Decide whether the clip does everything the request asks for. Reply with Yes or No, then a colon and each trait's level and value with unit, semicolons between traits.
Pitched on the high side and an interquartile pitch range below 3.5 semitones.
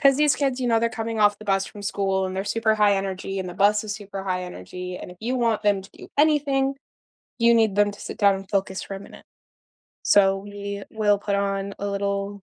Yes: high, 200 Hz; narrow, 2.4 semitones